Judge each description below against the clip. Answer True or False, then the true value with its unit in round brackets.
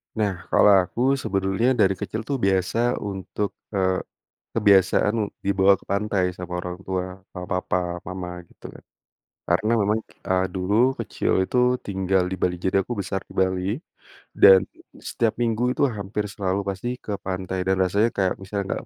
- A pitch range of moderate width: False (2.2 semitones)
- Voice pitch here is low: True (95 Hz)